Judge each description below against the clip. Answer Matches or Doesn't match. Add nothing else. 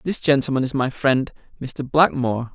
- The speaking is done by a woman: Doesn't match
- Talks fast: Doesn't match